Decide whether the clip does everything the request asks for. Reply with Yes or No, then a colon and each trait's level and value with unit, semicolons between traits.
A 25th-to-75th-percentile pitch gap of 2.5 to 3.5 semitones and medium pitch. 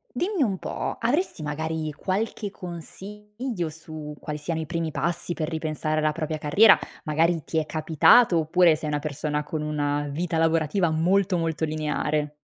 Yes: average, 2.8 semitones; medium, 160 Hz